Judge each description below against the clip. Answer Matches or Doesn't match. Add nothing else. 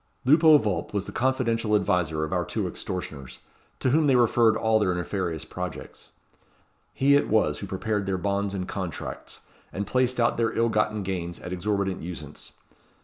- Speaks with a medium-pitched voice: Doesn't match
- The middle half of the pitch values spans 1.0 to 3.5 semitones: Doesn't match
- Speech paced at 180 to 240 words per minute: Doesn't match